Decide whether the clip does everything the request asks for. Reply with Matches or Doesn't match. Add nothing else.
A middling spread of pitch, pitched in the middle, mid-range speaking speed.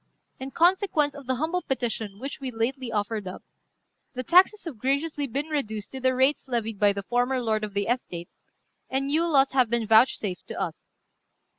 Doesn't match